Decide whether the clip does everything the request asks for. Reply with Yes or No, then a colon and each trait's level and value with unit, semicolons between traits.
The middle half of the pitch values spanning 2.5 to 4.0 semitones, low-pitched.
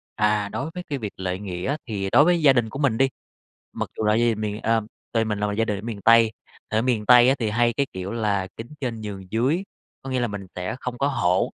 Yes: average, 3.3 semitones; low, 110 Hz